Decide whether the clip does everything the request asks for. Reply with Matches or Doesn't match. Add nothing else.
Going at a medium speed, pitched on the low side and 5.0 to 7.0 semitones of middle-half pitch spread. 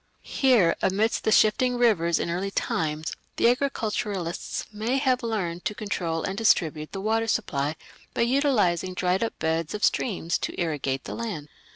Doesn't match